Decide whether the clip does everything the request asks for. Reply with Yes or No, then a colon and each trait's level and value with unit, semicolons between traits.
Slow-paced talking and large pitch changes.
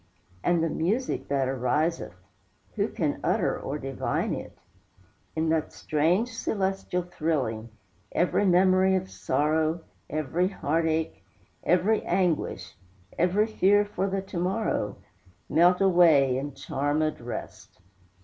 No: slow, 120 wpm; average, 4.3 semitones